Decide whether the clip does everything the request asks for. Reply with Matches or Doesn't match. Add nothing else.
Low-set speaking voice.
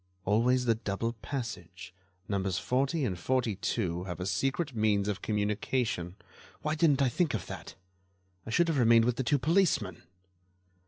Matches